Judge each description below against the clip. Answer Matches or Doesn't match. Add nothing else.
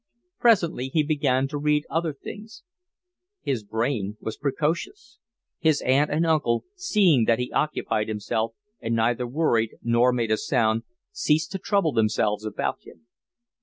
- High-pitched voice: Doesn't match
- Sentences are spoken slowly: Doesn't match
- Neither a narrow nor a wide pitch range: Doesn't match